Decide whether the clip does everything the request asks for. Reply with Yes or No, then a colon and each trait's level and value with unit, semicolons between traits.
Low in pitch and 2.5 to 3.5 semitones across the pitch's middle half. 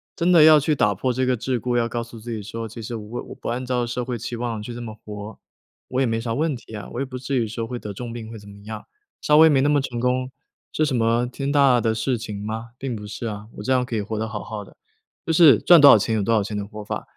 Yes: low, 120 Hz; average, 2.9 semitones